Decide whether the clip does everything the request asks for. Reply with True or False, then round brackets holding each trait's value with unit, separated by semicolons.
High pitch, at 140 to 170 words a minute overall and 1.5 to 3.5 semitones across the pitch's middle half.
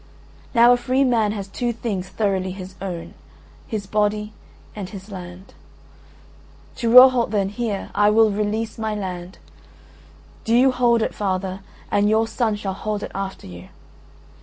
True (210 Hz; 155 wpm; 2.8 semitones)